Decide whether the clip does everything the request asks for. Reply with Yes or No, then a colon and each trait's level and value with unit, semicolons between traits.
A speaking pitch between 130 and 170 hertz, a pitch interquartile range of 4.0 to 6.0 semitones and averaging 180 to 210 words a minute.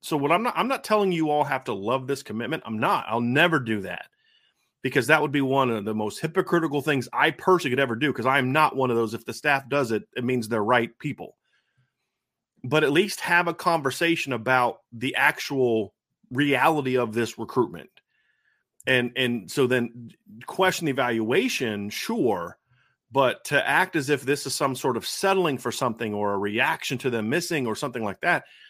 Yes: low, 135 Hz; average, 4.5 semitones; average, 200 wpm